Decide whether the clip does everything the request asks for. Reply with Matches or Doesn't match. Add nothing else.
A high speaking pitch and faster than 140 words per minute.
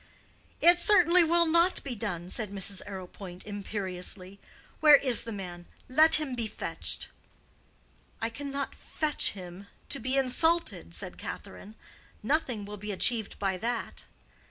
Doesn't match